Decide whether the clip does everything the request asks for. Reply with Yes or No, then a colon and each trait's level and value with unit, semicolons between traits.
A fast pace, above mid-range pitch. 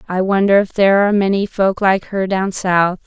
Yes: fast, 215 wpm; high, 195 Hz